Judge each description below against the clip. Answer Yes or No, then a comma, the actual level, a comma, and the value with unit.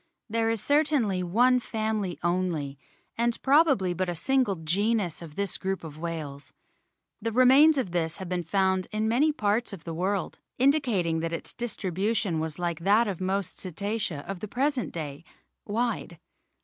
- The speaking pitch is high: Yes, high, 195 Hz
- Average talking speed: Yes, average, 160 wpm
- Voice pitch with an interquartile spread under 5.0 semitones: No, average, 5.3 semitones